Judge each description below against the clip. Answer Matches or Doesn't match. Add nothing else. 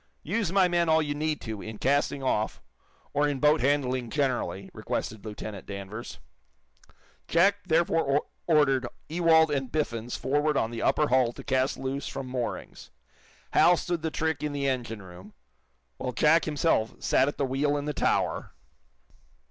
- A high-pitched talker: Doesn't match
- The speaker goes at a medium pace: Matches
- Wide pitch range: Doesn't match